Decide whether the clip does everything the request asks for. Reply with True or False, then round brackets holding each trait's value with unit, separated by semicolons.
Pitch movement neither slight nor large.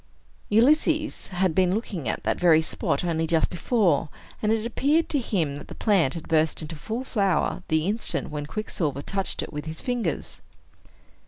False (5.9 semitones)